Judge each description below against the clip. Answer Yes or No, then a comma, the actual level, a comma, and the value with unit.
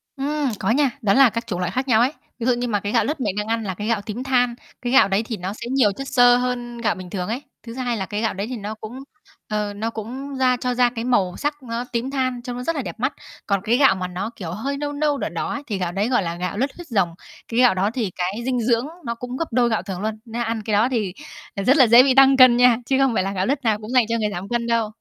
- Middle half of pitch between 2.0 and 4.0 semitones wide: Yes, average, 3.6 semitones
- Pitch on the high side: Yes, high, 235 Hz